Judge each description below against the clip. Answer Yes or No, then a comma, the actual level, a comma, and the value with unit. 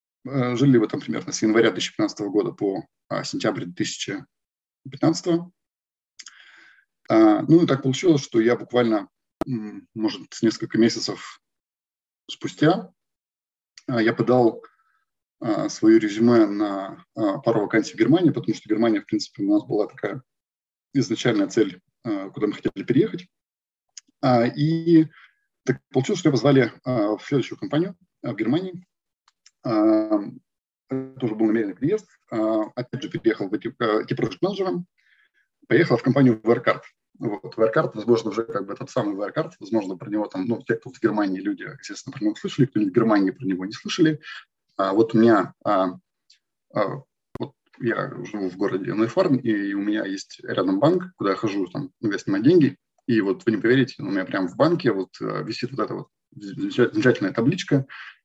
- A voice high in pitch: No, low, 135 Hz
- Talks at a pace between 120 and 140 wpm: No, average, 150 wpm